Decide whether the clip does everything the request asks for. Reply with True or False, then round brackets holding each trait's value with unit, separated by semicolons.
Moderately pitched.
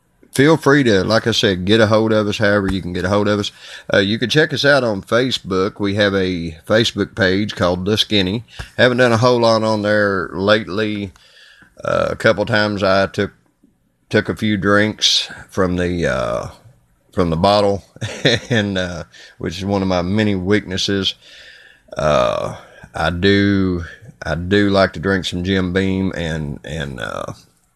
False (100 Hz)